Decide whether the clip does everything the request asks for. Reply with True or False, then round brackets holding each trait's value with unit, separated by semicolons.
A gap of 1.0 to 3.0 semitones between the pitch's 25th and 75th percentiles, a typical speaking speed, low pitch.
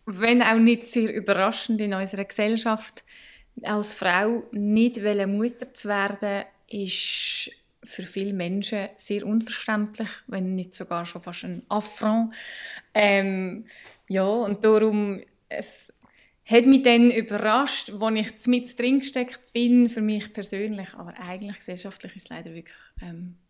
False (2.6 semitones; 135 wpm; 210 Hz)